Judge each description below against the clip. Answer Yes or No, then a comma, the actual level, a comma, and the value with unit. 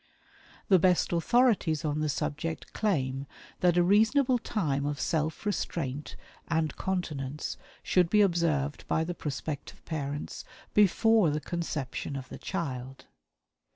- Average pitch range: Yes, average, 4.6 semitones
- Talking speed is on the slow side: Yes, slow, 125 wpm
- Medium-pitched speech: Yes, medium, 160 Hz